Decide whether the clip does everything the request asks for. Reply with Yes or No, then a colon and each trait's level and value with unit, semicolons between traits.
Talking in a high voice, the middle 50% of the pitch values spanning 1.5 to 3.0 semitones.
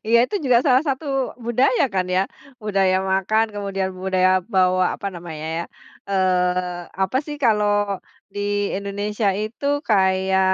Yes: high, 195 Hz; average, 2.7 semitones